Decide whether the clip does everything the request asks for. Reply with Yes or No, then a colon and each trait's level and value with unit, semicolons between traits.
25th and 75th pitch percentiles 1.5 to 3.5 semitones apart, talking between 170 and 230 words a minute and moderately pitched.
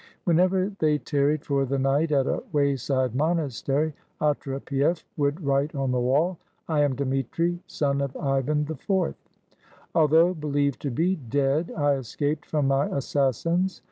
No: narrow, 2.6 semitones; average, 140 wpm; medium, 145 Hz